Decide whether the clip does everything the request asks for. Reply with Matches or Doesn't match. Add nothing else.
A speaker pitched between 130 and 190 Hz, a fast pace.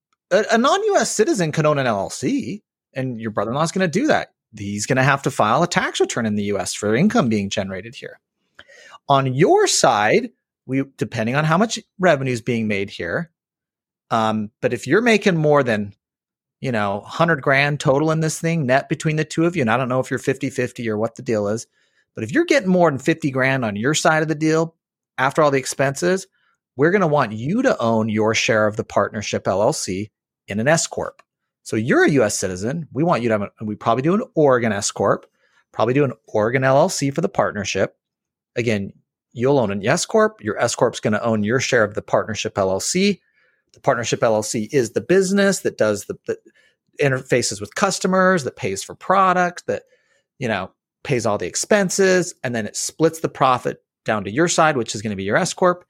Matches